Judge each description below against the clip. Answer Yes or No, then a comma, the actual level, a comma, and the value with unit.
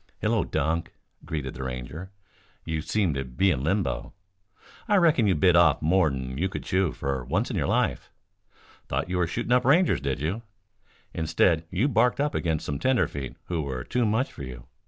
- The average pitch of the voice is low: Yes, very low, 85 Hz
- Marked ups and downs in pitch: Yes, wide, 7.1 semitones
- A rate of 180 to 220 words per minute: Yes, average, 185 wpm